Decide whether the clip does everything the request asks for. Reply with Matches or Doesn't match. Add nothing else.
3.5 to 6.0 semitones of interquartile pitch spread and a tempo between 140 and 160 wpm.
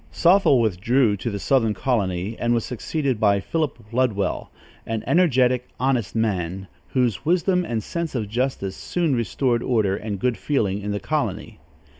Matches